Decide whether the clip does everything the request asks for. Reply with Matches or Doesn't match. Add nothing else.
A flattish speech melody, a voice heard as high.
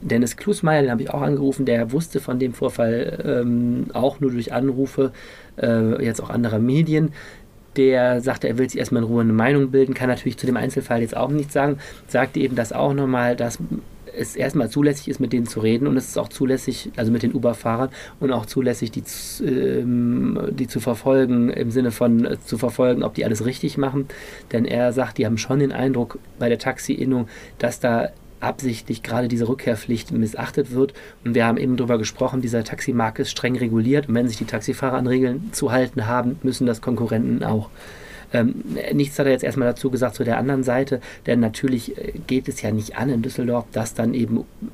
Doesn't match